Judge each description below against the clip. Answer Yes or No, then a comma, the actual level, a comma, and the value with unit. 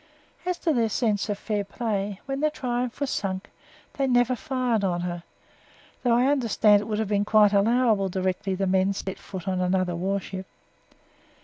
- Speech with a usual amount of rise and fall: Yes, average, 4.2 semitones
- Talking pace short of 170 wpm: No, average, 180 wpm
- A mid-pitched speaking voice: No, high, 205 Hz